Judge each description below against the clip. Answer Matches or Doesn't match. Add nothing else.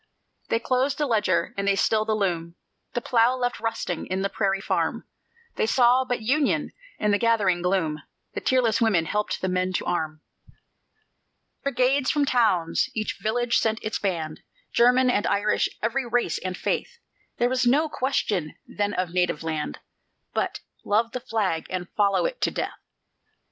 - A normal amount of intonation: Matches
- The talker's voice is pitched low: Doesn't match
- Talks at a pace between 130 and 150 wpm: Doesn't match